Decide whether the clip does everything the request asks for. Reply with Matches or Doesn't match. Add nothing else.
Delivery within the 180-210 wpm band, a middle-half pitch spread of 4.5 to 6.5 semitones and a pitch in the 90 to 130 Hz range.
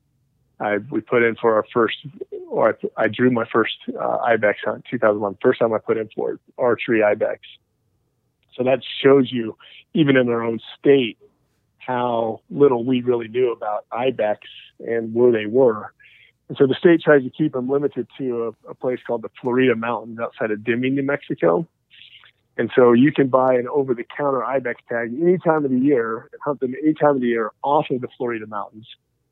Doesn't match